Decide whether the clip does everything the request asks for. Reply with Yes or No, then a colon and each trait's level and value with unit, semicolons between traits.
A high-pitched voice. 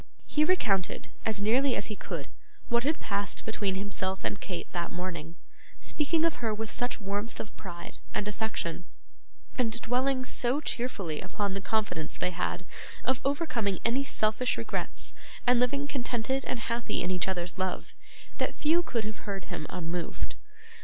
Yes: high, 215 Hz